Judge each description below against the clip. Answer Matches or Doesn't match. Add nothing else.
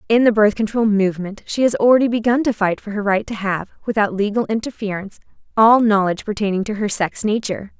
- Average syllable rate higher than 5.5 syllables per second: Matches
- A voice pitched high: Matches